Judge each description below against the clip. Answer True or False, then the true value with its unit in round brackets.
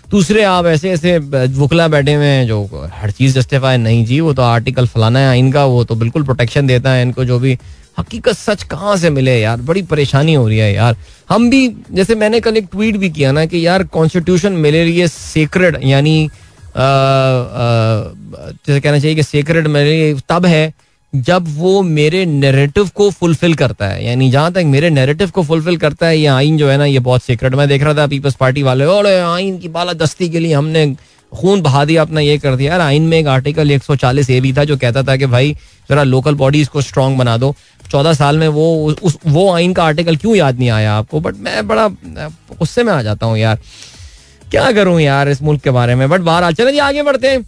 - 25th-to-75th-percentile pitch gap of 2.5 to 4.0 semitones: False (4.5 semitones)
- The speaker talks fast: True (215 wpm)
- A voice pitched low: False (145 Hz)